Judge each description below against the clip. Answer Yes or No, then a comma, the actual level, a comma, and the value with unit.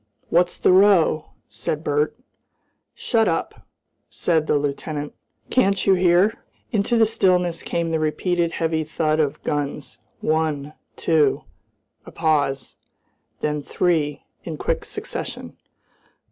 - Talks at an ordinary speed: No, slow, 120 wpm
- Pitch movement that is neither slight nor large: Yes, average, 3.2 semitones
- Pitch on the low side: No, medium, 160 Hz